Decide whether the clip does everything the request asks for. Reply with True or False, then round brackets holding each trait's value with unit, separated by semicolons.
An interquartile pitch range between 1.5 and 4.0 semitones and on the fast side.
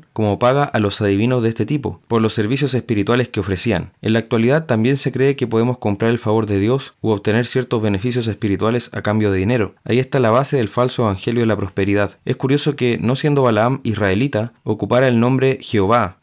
True (3.1 semitones; 210 wpm)